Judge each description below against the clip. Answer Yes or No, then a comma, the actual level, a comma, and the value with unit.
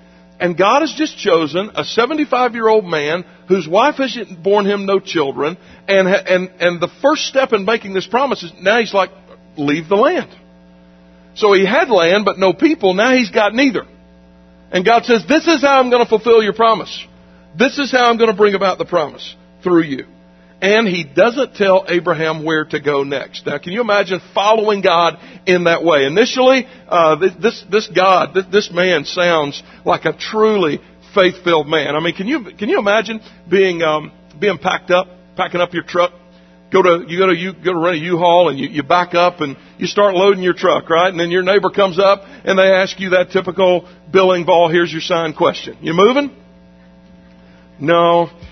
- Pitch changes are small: No, average, 3.9 semitones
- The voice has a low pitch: No, medium, 185 Hz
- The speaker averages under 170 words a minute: No, average, 200 wpm